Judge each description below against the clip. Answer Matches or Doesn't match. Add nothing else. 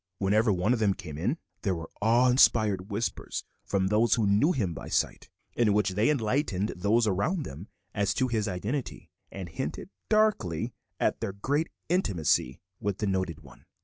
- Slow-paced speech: Doesn't match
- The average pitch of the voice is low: Matches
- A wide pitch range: Doesn't match